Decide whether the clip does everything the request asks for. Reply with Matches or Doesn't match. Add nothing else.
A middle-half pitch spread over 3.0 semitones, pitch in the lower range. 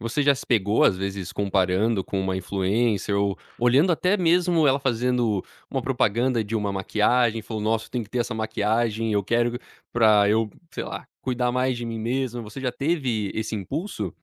Matches